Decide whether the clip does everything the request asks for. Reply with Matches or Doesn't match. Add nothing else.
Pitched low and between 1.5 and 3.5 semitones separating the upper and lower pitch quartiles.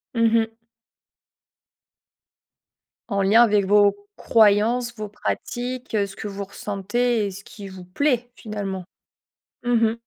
Doesn't match